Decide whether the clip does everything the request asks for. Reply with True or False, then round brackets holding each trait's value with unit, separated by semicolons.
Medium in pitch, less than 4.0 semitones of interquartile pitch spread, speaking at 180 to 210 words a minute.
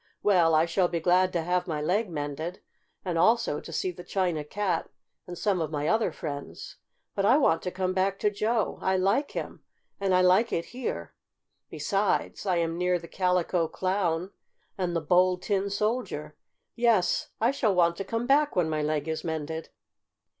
True (180 Hz; 3.3 semitones; 185 wpm)